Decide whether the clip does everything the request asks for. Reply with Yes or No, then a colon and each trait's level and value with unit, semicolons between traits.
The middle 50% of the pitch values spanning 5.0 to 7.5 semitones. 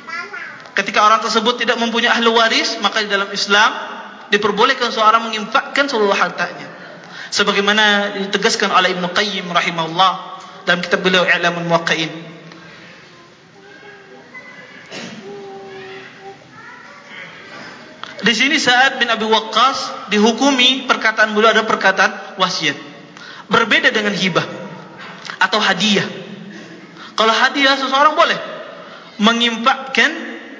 No: average, 3.9 semitones